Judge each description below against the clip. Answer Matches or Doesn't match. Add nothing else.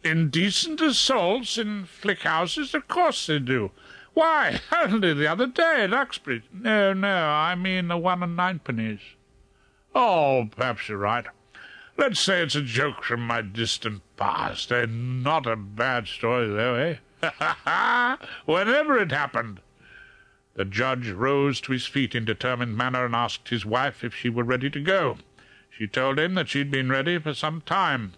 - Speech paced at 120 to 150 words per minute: Doesn't match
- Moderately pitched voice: Matches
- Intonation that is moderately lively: Doesn't match